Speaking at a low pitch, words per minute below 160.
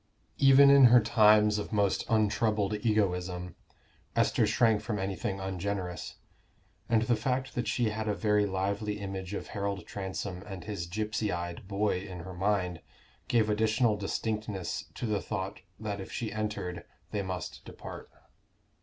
Yes: low, 105 Hz; average, 150 wpm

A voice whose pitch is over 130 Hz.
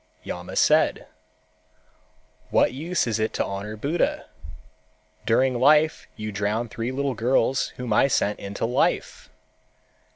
No: low, 115 Hz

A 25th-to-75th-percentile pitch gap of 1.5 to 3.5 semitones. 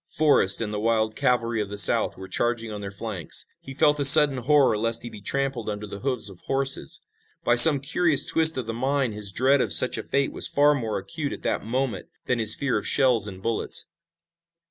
No: average, 4.5 semitones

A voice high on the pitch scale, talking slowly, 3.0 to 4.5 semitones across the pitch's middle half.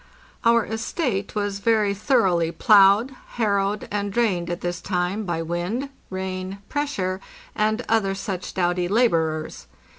Yes: high, 200 Hz; slow, 130 wpm; average, 3.7 semitones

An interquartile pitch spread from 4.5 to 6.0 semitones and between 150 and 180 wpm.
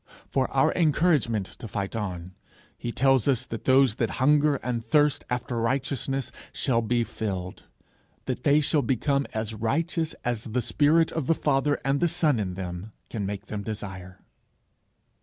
Yes: average, 5.1 semitones; average, 160 wpm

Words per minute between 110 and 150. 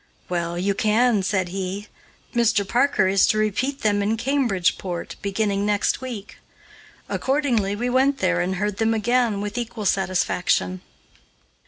Yes: average, 140 wpm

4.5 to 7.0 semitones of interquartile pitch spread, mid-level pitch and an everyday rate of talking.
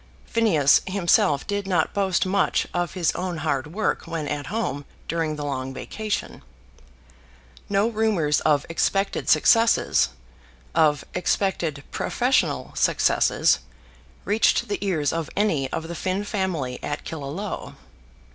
No: average, 5.3 semitones; medium, 170 Hz; slow, 125 wpm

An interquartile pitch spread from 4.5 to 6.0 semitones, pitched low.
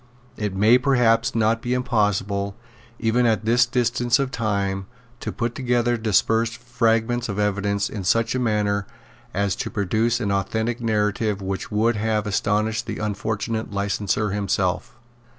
No: narrow, 2.5 semitones; low, 110 Hz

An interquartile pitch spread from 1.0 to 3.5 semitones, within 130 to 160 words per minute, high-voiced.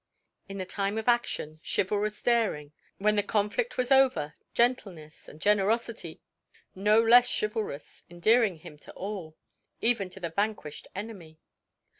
No: average, 4.7 semitones; slow, 135 wpm; high, 205 Hz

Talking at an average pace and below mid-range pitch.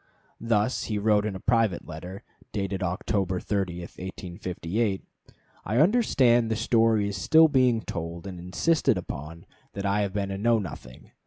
Yes: average, 155 wpm; low, 100 Hz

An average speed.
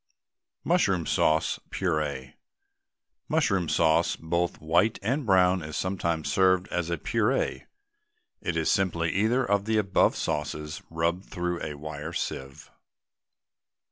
No: slow, 120 wpm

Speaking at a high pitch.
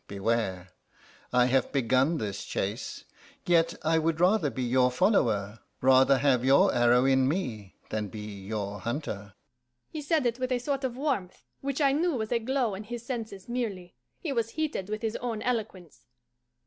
No: medium, 165 Hz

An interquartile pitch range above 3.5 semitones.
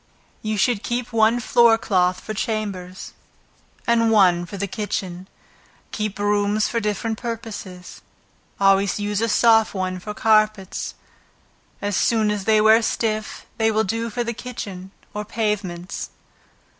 No: narrow, 2.4 semitones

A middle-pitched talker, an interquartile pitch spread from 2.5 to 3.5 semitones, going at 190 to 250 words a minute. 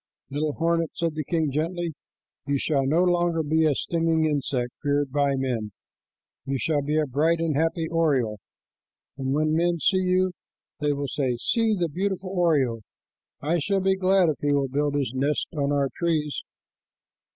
No: medium, 155 Hz; average, 3.1 semitones; average, 175 wpm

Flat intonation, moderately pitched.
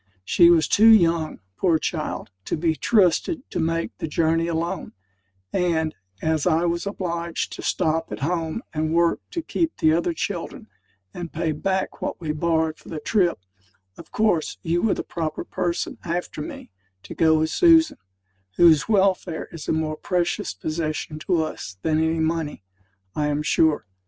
Yes: narrow, 1.9 semitones; medium, 165 Hz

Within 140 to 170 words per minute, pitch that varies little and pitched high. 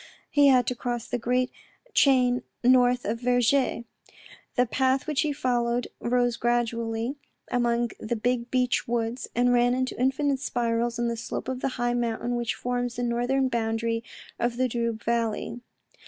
Yes: average, 160 wpm; narrow, 1.2 semitones; high, 245 Hz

